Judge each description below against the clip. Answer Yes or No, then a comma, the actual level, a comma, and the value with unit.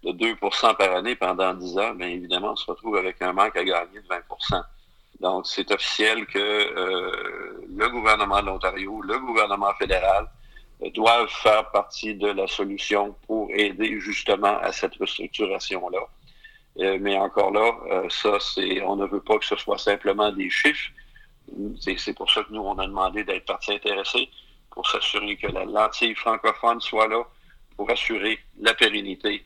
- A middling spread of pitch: Yes, average, 3.4 semitones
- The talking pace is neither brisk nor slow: Yes, average, 175 wpm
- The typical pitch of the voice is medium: No, low, 105 Hz